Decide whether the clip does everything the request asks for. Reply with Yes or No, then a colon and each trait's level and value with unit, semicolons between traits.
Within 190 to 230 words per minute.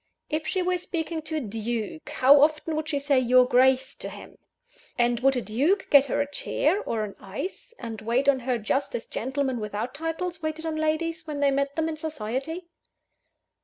Yes: average, 200 wpm